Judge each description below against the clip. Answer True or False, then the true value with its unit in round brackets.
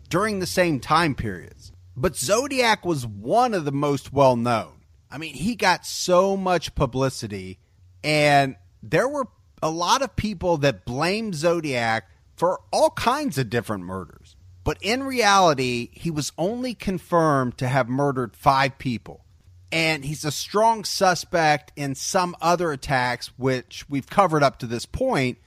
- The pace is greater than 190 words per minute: False (155 wpm)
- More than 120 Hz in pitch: True (140 Hz)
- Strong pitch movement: True (6.7 semitones)